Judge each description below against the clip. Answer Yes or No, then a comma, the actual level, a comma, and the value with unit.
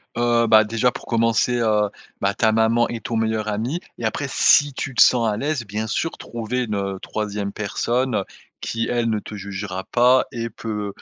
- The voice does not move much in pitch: Yes, narrow, 2.3 semitones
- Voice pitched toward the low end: Yes, low, 115 Hz